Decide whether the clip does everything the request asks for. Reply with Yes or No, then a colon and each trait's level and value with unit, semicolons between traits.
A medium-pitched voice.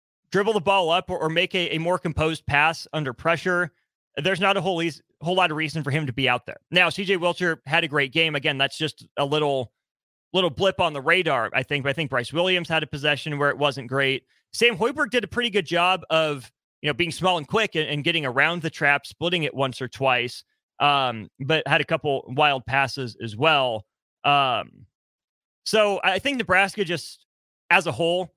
Yes: medium, 160 Hz